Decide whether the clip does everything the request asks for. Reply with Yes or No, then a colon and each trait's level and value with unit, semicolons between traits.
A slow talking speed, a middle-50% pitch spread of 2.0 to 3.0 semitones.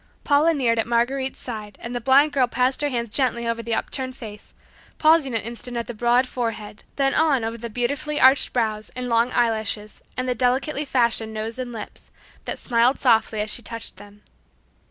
No: average, 195 wpm; narrow, 2.6 semitones